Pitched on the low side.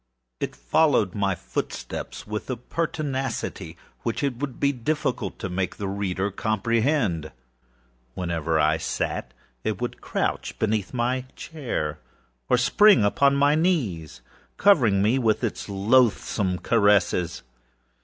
Yes: low, 110 Hz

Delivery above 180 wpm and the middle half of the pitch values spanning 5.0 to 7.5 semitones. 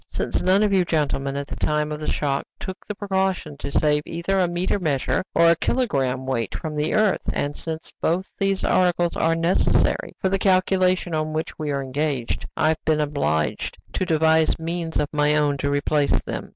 No: average, 200 wpm; average, 3.9 semitones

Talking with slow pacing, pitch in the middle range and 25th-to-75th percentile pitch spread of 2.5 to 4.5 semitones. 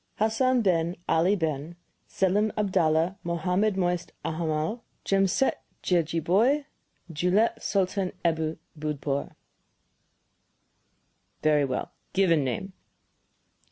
Yes: slow, 80 wpm; medium, 180 Hz; average, 3.7 semitones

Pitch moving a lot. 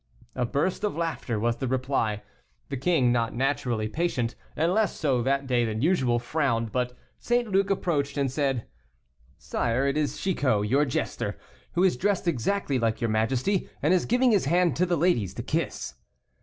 Yes: wide, 6.5 semitones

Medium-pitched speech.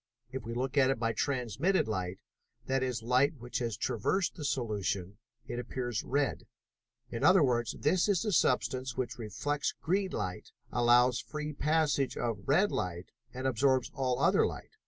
No: low, 130 Hz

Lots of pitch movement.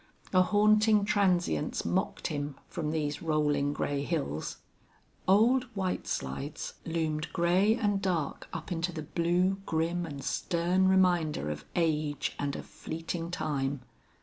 No: average, 4.0 semitones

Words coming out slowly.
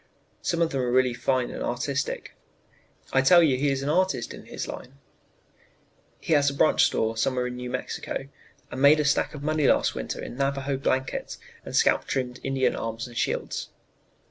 No: average, 195 wpm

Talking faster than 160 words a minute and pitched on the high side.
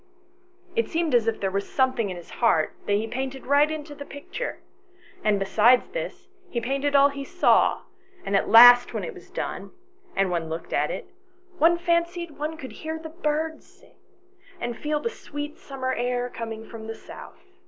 Yes: average, 185 wpm; very high, 265 Hz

